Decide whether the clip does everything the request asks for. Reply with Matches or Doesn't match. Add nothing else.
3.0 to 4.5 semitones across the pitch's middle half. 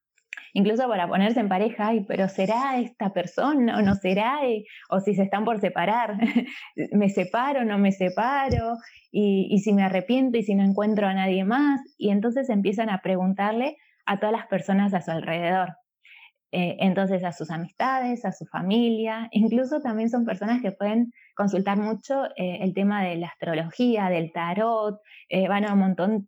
Matches